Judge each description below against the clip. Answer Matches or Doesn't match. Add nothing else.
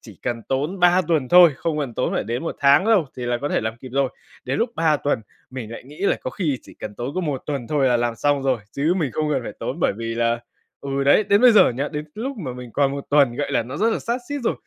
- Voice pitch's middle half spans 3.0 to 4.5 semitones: Doesn't match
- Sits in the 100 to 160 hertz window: Matches